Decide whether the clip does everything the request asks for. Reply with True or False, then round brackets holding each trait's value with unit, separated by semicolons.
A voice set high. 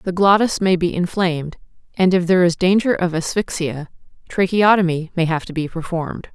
False (175 Hz)